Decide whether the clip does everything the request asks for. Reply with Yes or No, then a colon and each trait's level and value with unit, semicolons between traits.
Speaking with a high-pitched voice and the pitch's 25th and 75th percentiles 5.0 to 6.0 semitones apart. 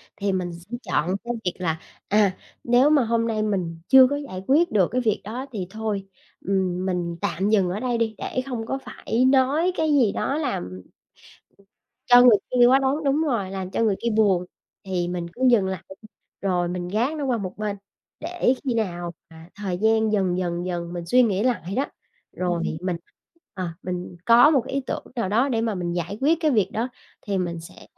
Yes: high, 210 Hz; wide, 5.4 semitones